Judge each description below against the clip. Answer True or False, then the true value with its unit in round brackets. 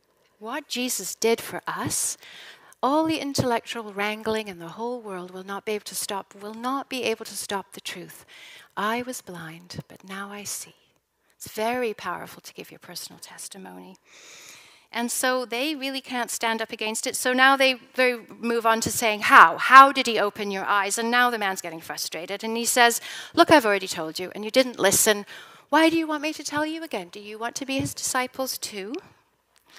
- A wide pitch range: False (4.4 semitones)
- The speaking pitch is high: True (230 Hz)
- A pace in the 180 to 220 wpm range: True (205 wpm)